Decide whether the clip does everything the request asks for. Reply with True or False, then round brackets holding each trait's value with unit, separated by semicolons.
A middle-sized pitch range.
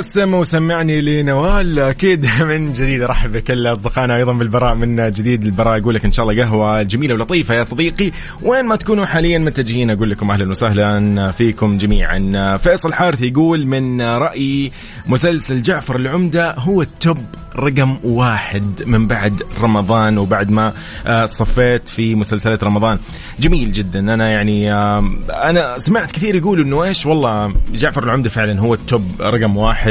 False (5.9 semitones)